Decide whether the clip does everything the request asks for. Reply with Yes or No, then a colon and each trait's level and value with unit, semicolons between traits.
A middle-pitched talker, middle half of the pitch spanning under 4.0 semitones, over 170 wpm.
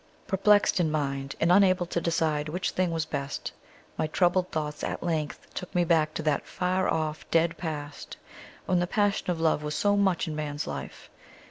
Yes: medium, 165 Hz; average, 3.0 semitones; average, 190 wpm